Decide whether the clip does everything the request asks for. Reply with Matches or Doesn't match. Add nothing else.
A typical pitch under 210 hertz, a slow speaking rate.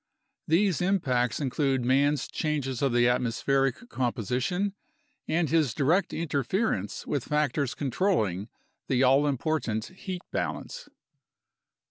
Matches